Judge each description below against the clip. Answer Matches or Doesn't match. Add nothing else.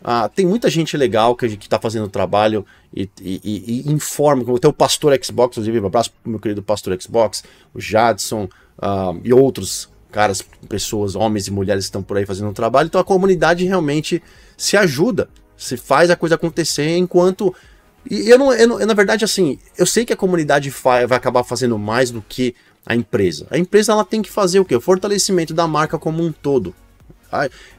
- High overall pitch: Doesn't match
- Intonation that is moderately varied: Doesn't match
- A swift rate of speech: Matches